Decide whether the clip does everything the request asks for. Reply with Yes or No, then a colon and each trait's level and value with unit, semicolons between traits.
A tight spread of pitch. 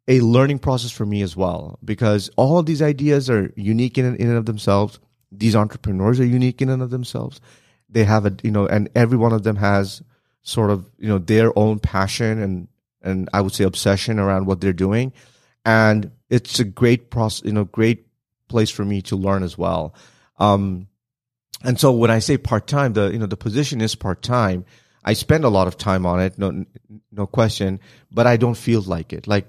No: average, 3.7 semitones